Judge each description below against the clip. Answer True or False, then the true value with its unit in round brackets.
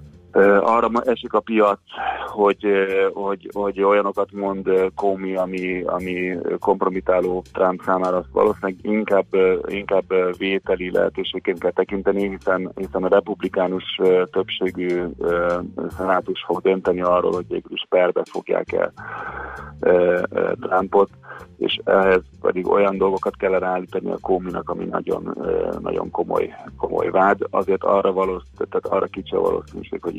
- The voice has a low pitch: True (95 Hz)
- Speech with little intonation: False (3.7 semitones)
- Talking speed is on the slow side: False (120 wpm)